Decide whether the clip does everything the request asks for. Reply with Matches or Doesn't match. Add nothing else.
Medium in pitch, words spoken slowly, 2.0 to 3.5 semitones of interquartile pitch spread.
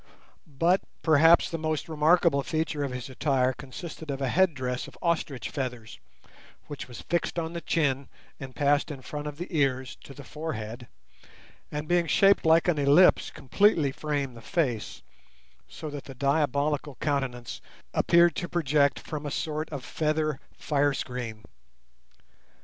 Doesn't match